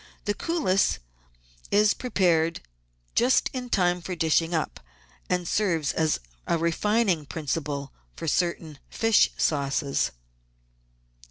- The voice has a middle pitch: Yes, medium, 170 Hz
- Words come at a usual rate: No, slow, 105 wpm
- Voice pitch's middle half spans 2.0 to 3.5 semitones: No, average, 4.8 semitones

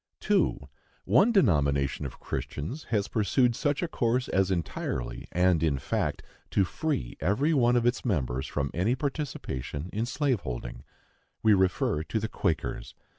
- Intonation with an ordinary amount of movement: No, wide, 8.9 semitones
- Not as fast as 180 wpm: Yes, average, 150 wpm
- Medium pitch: No, low, 100 Hz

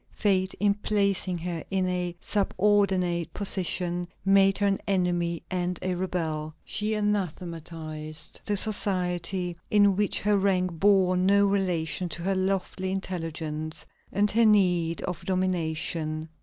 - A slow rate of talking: Yes, slow, 130 wpm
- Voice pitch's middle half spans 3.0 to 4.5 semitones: No, narrow, 2.6 semitones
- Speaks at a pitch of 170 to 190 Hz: Yes, medium, 185 Hz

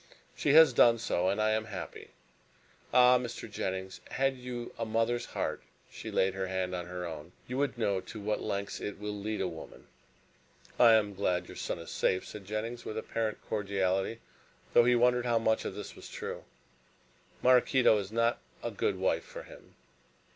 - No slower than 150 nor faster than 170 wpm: No, average, 185 wpm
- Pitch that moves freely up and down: No, average, 4.0 semitones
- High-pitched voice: No, low, 110 Hz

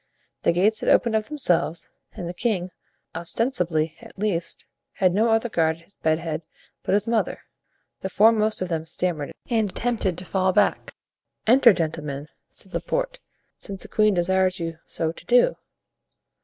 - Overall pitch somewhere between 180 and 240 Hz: Yes, medium, 185 Hz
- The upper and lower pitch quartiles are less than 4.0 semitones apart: No, average, 4.7 semitones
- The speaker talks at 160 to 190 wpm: Yes, average, 165 wpm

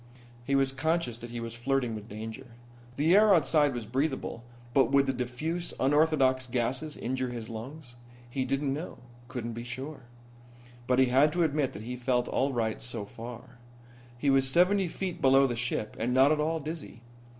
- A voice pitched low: Yes, low, 130 Hz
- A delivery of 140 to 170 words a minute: No, average, 185 wpm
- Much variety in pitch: No, average, 3.6 semitones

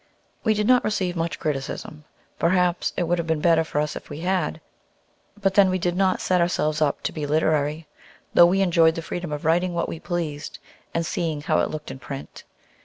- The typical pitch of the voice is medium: Yes, medium, 165 Hz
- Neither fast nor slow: No, fast, 210 wpm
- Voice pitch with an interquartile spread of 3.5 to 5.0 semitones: No, average, 2.8 semitones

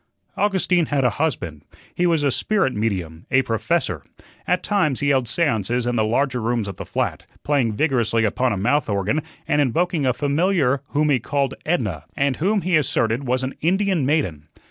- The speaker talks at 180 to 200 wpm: Yes, average, 185 wpm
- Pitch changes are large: Yes, wide, 5.7 semitones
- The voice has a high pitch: No, low, 135 Hz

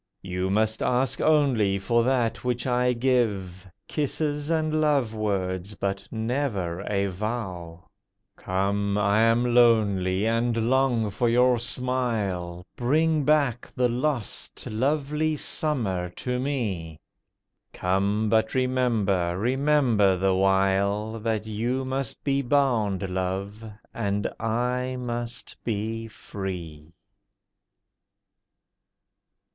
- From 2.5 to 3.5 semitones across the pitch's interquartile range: No, average, 4.5 semitones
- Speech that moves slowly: Yes, slow, 105 wpm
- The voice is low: Yes, low, 115 Hz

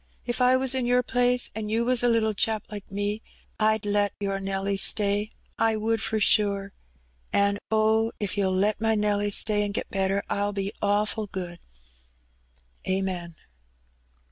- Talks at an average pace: Yes, average, 165 wpm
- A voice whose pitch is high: Yes, high, 210 Hz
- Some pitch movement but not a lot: No, narrow, 1.8 semitones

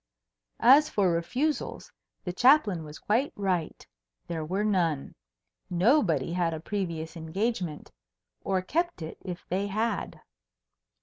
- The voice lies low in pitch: No, medium, 185 Hz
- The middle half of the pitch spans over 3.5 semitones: Yes, average, 4.8 semitones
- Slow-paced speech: Yes, slow, 120 wpm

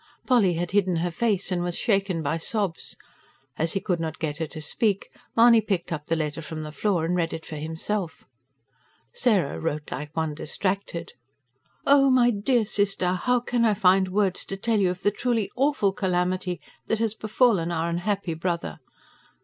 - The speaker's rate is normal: Yes, average, 180 wpm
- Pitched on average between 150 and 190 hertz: Yes, medium, 185 Hz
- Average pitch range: Yes, average, 4.3 semitones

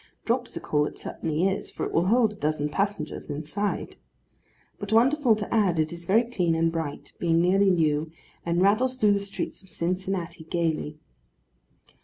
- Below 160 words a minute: No, average, 165 wpm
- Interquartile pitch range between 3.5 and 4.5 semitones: Yes, average, 4.2 semitones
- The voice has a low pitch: No, medium, 180 Hz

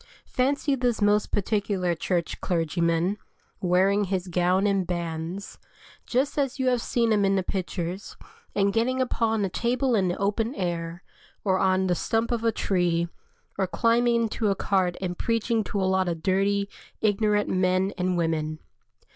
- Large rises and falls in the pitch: No, average, 3.9 semitones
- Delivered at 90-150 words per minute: No, average, 165 wpm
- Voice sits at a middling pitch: No, high, 195 Hz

